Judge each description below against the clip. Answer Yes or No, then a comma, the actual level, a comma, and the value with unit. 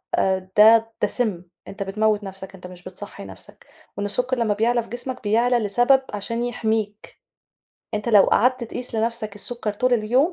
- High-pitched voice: Yes, high, 220 Hz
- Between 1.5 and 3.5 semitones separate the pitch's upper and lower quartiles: Yes, average, 3.0 semitones